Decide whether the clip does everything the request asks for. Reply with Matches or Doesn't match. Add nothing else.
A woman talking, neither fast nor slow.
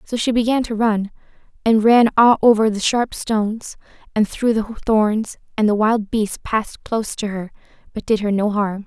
Matches